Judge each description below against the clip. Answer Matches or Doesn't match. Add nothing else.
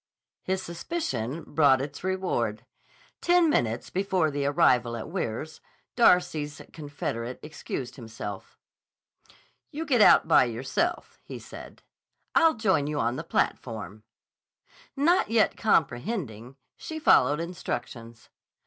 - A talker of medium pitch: Matches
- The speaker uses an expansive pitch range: Matches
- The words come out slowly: Matches